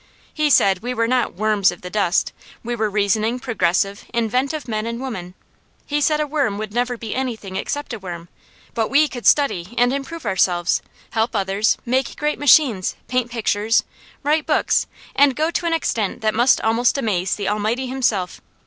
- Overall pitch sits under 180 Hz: No, high, 230 Hz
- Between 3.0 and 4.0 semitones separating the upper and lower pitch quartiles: No, average, 4.5 semitones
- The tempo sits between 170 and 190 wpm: Yes, average, 180 wpm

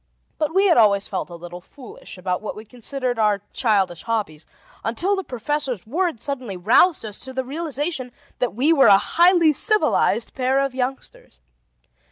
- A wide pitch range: Yes, wide, 6.1 semitones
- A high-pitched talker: Yes, very high, 250 Hz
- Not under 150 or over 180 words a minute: Yes, average, 170 wpm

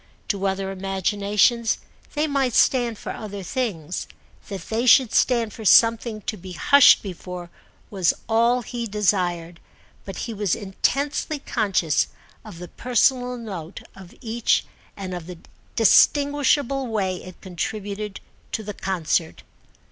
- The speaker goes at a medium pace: No, slow, 130 wpm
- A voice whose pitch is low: No, high, 210 Hz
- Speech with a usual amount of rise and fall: Yes, average, 4.2 semitones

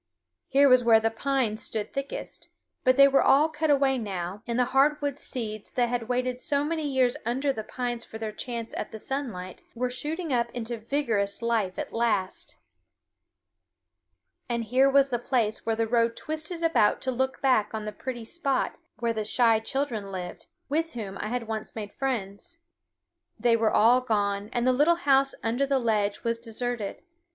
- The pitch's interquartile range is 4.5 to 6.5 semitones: No, average, 3.6 semitones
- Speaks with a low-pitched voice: No, high, 240 Hz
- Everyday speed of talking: Yes, average, 180 wpm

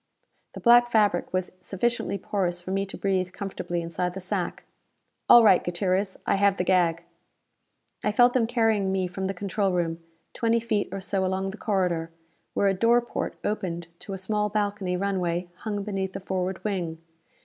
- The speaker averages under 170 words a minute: No, average, 180 wpm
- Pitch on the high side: Yes, high, 195 Hz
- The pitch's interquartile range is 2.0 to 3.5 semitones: Yes, narrow, 2.5 semitones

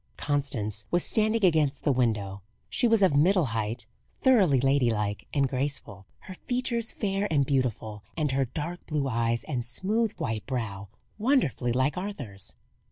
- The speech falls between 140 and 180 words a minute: Yes, average, 150 wpm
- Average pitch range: No, wide, 8.2 semitones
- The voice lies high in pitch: No, medium, 140 Hz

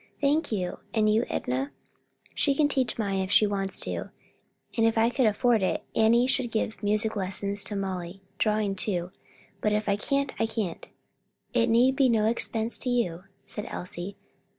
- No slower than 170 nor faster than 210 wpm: Yes, average, 175 wpm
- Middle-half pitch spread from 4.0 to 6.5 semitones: No, average, 3.4 semitones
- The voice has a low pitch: No, high, 215 Hz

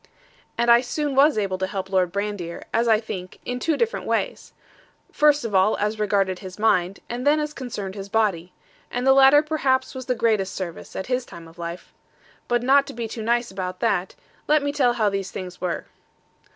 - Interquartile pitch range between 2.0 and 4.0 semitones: No, wide, 5.4 semitones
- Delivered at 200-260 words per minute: Yes, fast, 205 wpm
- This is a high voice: Yes, high, 220 Hz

